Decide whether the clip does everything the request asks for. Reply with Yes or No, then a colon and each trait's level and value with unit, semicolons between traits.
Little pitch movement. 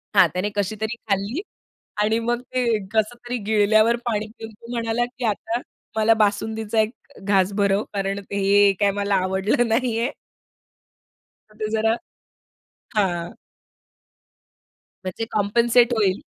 Yes: narrow, 2.3 semitones